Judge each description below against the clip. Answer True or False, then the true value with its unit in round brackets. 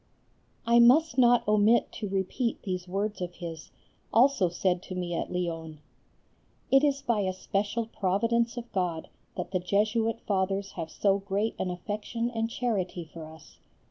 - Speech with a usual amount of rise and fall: True (4.3 semitones)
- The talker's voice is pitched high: True (200 Hz)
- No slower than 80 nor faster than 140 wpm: False (160 wpm)